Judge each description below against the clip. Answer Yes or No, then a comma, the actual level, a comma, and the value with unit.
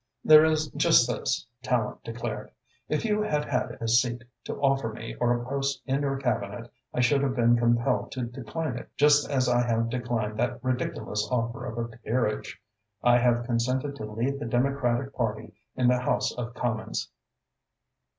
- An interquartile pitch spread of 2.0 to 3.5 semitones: Yes, average, 2.7 semitones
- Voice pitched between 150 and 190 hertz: No, low, 120 Hz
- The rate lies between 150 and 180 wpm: Yes, average, 175 wpm